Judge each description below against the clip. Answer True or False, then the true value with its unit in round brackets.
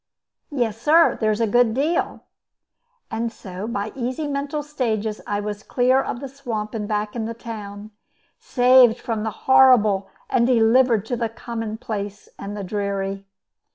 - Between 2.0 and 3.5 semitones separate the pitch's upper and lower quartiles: True (3.2 semitones)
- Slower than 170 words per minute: True (155 wpm)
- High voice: True (225 Hz)